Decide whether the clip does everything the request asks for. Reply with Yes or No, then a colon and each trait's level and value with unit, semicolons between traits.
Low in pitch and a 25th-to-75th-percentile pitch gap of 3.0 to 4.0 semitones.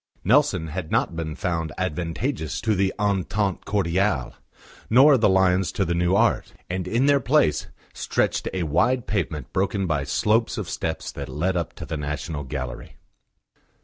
No: very low, 90 Hz; average, 4.5 semitones